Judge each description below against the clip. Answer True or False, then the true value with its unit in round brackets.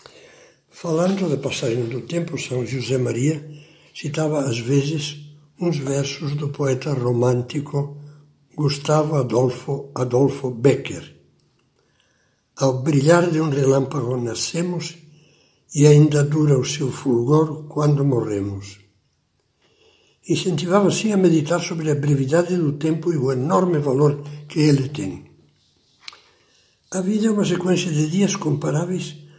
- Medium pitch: True (150 Hz)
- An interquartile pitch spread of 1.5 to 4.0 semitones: True (3.2 semitones)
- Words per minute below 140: True (120 wpm)